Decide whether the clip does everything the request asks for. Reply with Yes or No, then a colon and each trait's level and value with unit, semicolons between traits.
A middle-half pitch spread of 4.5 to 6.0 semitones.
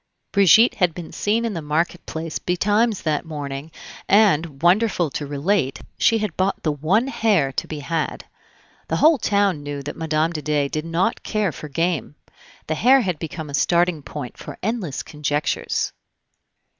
Yes: average, 5.3 semitones